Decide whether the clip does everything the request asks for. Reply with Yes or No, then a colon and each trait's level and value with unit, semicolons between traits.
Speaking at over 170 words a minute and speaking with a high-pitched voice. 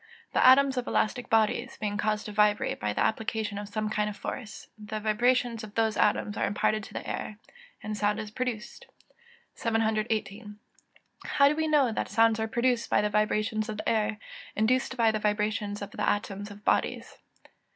Yes: average, 190 wpm; high, 215 Hz